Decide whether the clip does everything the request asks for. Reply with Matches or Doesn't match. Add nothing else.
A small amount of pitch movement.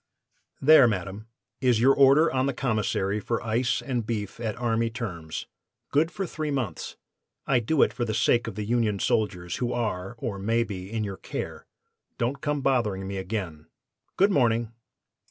Doesn't match